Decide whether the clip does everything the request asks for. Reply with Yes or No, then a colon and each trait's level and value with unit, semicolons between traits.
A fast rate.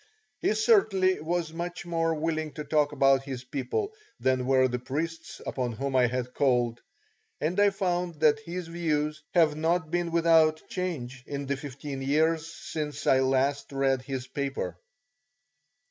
No: average, 155 wpm